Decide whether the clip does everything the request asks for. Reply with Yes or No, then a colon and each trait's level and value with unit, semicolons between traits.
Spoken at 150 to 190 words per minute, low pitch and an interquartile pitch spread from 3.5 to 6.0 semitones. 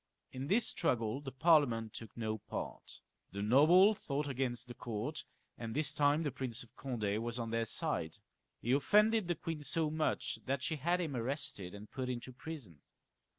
Yes: average, 180 wpm; low, 130 Hz; average, 5.0 semitones